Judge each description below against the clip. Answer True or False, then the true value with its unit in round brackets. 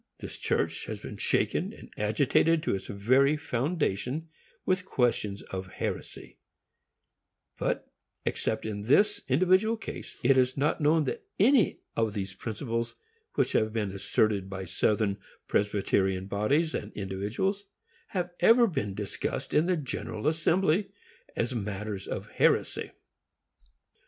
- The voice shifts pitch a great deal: True (8.1 semitones)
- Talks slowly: True (130 wpm)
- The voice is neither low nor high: False (120 Hz)